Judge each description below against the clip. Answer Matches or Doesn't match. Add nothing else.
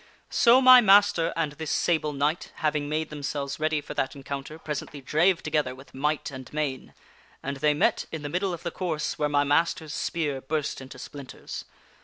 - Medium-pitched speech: Matches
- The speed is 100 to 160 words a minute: Doesn't match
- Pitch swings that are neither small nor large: Doesn't match